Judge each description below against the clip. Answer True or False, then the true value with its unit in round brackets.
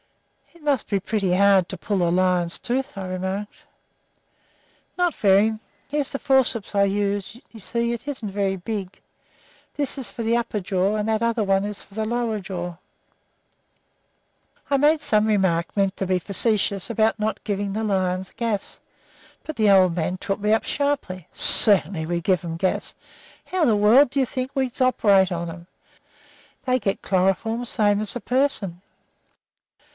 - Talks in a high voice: True (205 Hz)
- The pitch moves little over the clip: False (3.8 semitones)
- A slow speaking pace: False (170 wpm)